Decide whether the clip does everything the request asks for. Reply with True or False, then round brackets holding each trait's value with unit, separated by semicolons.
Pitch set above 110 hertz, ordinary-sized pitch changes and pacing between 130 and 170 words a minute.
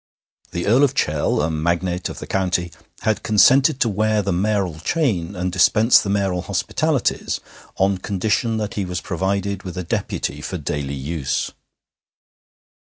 False (95 Hz; 3.5 semitones; 155 wpm)